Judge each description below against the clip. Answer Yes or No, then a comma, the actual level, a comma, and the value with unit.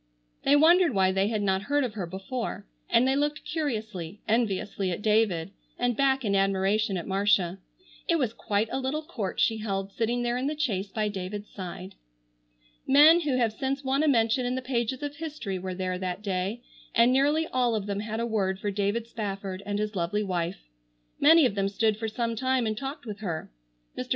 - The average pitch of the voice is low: No, high, 220 Hz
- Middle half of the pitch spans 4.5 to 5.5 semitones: Yes, average, 4.9 semitones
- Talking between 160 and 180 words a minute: No, fast, 205 wpm